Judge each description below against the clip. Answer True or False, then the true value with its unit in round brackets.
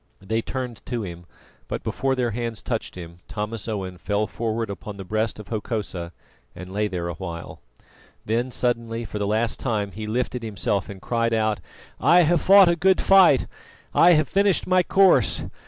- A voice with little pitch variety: False (3.9 semitones)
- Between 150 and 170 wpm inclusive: False (180 wpm)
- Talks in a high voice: False (110 Hz)